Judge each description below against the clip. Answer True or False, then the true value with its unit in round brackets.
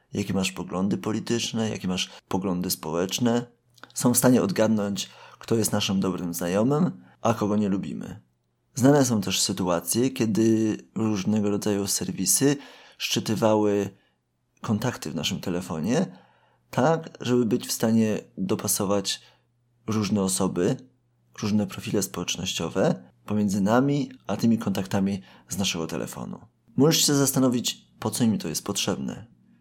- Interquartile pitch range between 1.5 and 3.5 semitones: False (4.0 semitones)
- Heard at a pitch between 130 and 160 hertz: False (105 Hz)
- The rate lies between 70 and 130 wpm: True (125 wpm)